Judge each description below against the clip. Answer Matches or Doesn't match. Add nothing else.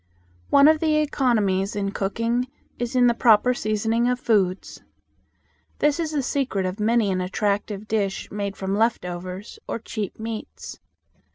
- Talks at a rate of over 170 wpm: Doesn't match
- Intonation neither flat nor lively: Matches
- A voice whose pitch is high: Matches